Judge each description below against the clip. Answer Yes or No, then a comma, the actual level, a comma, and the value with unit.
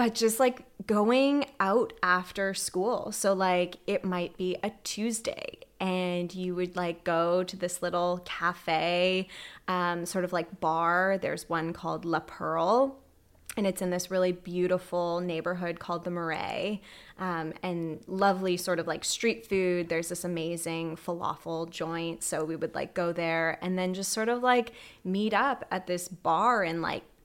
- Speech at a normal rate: Yes, average, 165 wpm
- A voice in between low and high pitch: Yes, medium, 180 Hz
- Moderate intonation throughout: No, narrow, 2.2 semitones